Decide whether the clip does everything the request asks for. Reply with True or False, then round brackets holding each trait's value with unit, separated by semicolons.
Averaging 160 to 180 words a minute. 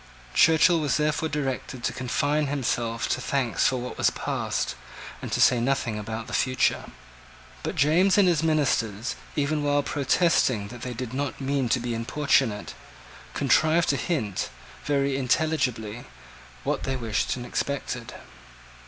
False (145 wpm)